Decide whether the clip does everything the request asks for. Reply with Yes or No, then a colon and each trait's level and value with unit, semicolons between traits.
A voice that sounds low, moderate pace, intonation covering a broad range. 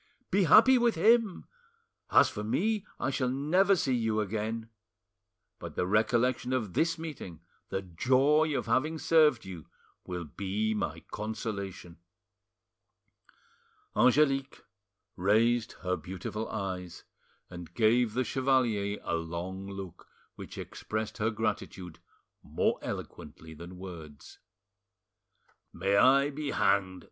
No: low, 110 Hz; slow, 115 wpm; wide, 6.4 semitones